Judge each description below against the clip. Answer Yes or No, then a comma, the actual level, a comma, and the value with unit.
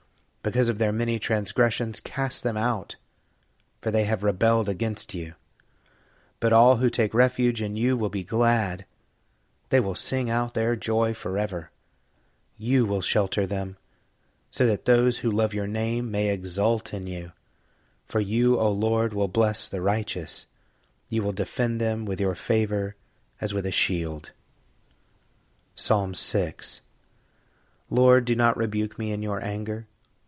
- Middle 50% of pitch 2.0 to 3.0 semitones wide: Yes, average, 2.7 semitones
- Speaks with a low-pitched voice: Yes, low, 110 Hz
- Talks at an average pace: Yes, average, 150 wpm